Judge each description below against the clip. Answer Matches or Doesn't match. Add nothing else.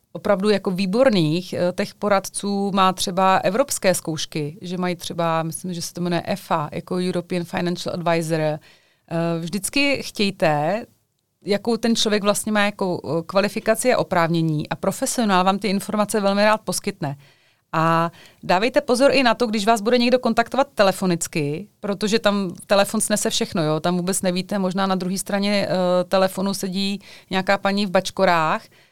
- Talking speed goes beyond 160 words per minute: Doesn't match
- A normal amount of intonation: Matches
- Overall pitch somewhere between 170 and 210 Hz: Matches